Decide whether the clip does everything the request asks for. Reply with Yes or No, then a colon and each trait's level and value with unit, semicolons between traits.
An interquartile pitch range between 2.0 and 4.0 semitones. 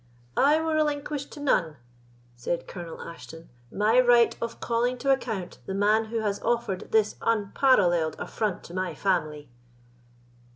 No: wide, 5.4 semitones